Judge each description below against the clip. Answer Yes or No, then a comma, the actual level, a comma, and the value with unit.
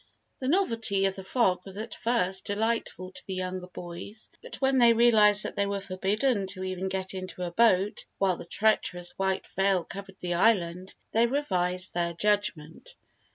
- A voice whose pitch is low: No, high, 195 Hz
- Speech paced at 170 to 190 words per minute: Yes, average, 175 wpm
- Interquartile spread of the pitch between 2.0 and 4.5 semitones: Yes, average, 3.3 semitones